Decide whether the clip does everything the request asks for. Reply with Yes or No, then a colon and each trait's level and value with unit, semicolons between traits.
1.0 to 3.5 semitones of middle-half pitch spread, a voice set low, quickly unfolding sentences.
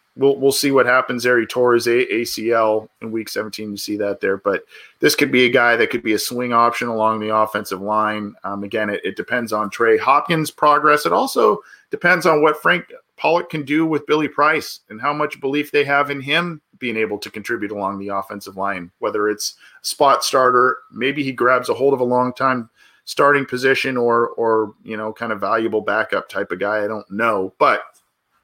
No: average, 4.6 semitones; low, 115 Hz; fast, 210 wpm